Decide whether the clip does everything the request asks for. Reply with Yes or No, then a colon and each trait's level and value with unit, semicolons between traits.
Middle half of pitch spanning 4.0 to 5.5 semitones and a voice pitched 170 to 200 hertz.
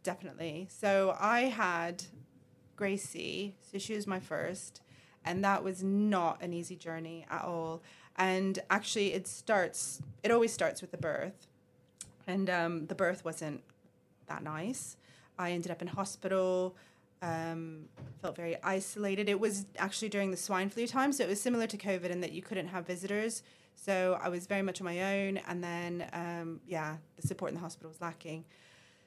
No: average, 2.8 semitones; medium, 185 Hz